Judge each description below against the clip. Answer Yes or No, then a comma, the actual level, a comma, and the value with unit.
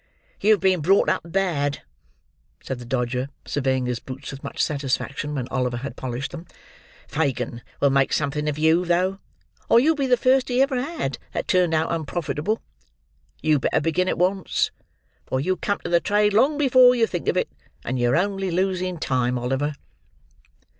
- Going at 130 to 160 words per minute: No, average, 175 wpm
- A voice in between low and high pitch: Yes, medium, 160 Hz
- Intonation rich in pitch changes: Yes, wide, 6.3 semitones